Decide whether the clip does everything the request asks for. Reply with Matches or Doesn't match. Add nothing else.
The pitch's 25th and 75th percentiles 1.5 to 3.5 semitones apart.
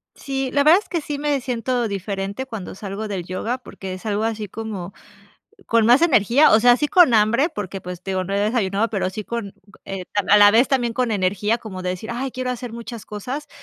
Doesn't match